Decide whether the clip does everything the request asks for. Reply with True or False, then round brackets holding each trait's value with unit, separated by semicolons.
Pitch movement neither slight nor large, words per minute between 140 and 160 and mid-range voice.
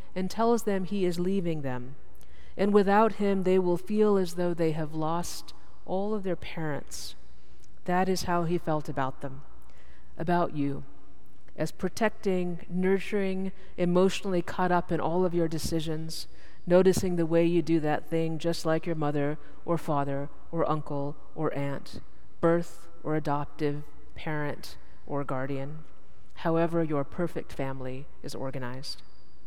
True (4.1 semitones; 145 wpm; 165 Hz)